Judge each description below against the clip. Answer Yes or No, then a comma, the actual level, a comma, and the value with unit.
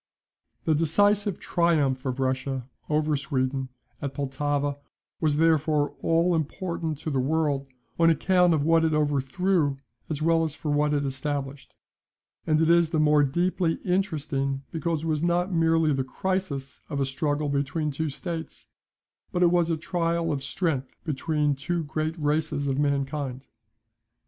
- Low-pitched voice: No, medium, 150 Hz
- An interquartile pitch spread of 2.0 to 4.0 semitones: Yes, average, 2.8 semitones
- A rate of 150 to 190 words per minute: Yes, average, 155 wpm